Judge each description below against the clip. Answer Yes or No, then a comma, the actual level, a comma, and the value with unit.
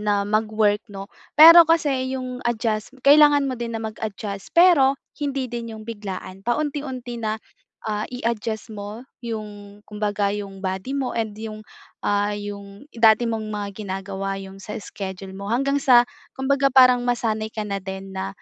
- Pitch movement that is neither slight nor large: Yes, average, 3.8 semitones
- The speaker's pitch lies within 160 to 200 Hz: No, high, 220 Hz